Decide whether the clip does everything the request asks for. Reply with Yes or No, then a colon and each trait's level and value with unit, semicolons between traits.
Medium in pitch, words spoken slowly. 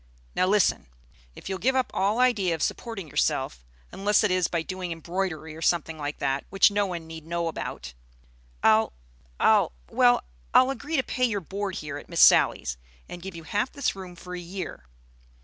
No: medium, 180 Hz; average, 190 wpm